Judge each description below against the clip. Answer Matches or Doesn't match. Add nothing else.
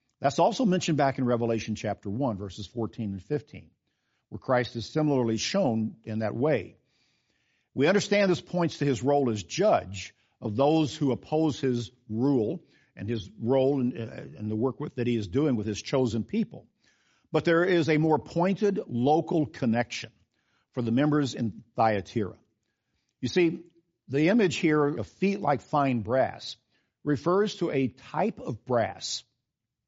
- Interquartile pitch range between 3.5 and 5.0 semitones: Doesn't match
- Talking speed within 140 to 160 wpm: Matches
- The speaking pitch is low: Matches